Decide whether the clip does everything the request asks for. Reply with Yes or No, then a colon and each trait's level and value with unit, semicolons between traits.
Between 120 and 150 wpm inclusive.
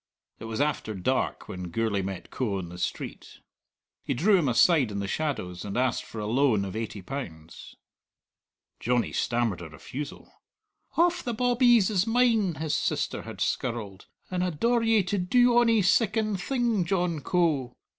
No: average, 165 wpm